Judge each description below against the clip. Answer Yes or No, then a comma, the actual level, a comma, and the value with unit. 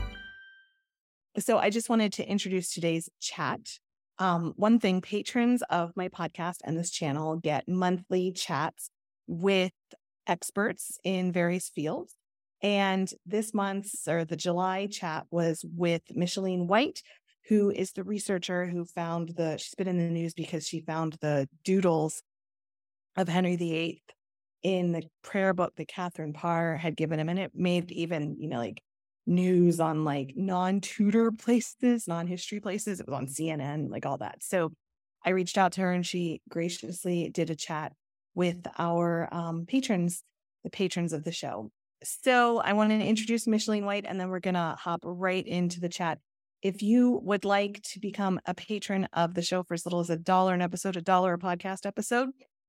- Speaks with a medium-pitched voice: Yes, medium, 180 Hz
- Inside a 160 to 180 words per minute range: Yes, average, 170 wpm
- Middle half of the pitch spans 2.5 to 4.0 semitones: Yes, average, 3.1 semitones